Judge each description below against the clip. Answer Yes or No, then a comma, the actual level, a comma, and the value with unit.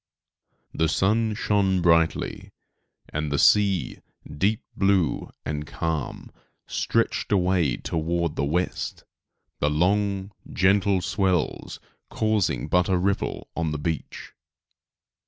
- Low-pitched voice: Yes, very low, 90 Hz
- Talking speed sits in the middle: No, slow, 105 wpm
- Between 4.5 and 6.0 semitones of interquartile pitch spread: No, average, 3.7 semitones